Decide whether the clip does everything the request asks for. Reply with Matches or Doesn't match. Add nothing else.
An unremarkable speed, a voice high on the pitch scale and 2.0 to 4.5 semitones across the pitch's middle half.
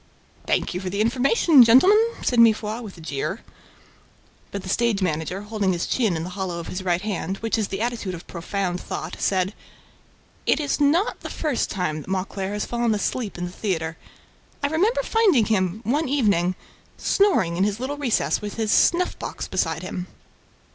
Doesn't match